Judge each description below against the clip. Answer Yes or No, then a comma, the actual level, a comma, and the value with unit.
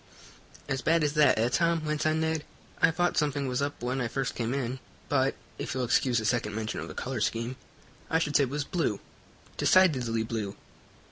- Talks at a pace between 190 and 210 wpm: Yes, fast, 205 wpm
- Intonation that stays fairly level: No, average, 4.4 semitones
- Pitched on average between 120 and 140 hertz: Yes, low, 135 Hz